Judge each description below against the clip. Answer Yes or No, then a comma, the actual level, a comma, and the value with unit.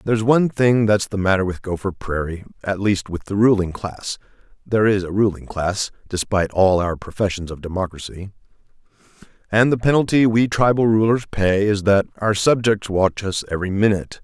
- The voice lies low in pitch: Yes, low, 100 Hz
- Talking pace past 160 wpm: Yes, average, 175 wpm